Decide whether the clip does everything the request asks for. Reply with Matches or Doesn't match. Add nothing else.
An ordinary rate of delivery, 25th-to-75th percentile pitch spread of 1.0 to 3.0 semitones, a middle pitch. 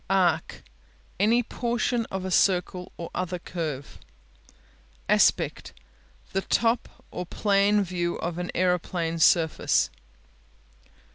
Doesn't match